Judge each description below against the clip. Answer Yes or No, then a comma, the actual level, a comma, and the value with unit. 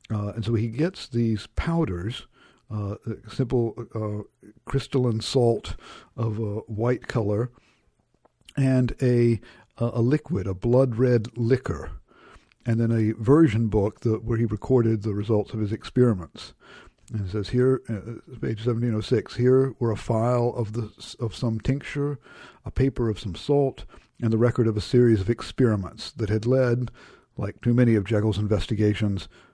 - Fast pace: No, average, 150 wpm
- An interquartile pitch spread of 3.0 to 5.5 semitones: No, narrow, 2.4 semitones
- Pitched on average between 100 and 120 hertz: Yes, low, 115 Hz